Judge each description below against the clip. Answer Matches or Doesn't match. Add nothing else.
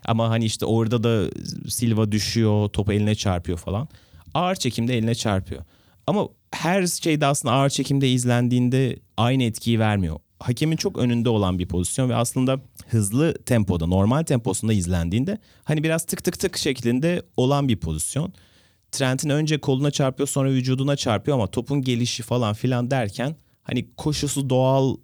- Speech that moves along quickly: Matches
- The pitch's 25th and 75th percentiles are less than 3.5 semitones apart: Doesn't match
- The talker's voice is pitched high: Doesn't match